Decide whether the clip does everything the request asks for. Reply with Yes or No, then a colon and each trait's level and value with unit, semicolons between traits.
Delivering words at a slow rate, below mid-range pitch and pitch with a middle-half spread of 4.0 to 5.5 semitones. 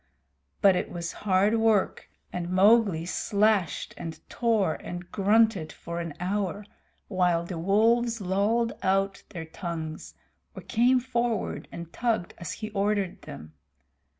No: slow, 130 wpm; high, 195 Hz; average, 4.3 semitones